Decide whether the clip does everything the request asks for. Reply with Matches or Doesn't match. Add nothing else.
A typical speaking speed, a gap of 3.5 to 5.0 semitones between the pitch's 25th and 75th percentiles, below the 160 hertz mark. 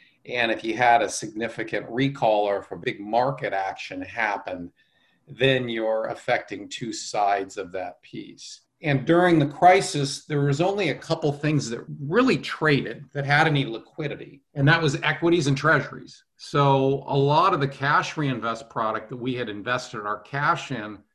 Matches